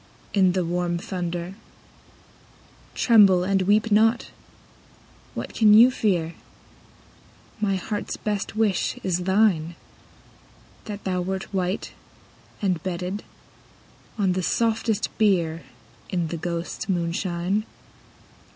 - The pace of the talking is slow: Yes, slow, 110 wpm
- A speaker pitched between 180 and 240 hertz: Yes, high, 190 Hz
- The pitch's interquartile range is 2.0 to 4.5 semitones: Yes, average, 3.0 semitones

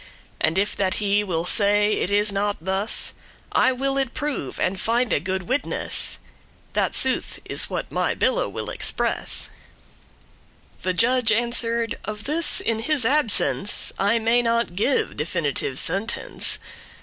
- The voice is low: No, high, 215 Hz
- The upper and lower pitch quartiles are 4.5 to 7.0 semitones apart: No, average, 4.0 semitones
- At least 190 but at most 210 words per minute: No, average, 140 wpm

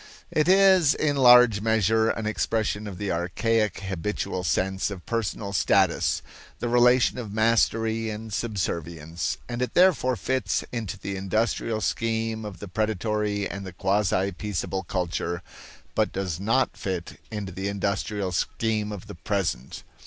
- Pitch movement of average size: Yes, average, 3.0 semitones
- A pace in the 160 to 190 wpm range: No, average, 145 wpm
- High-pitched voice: No, low, 105 Hz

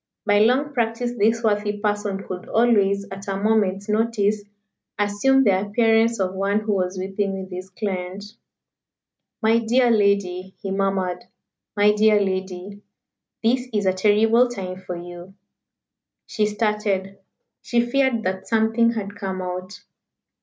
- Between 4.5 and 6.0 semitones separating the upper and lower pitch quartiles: No, average, 2.7 semitones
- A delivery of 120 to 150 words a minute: Yes, average, 140 wpm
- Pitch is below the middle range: No, high, 205 Hz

